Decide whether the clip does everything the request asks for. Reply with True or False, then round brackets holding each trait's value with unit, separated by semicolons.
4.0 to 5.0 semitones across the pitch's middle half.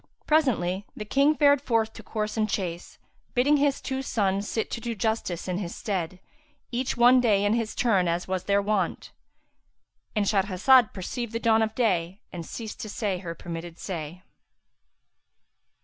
True (4.4 semitones)